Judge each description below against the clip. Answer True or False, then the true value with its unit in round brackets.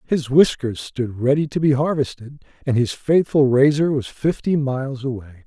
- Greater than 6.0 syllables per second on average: False (4.9 syllables/s)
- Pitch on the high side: False (135 Hz)